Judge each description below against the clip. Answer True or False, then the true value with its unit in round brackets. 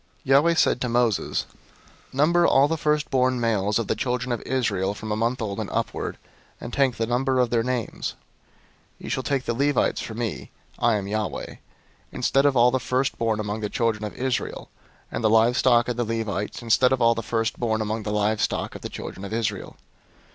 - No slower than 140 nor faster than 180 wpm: False (200 wpm)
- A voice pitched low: True (120 Hz)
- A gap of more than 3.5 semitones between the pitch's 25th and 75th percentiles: False (2.8 semitones)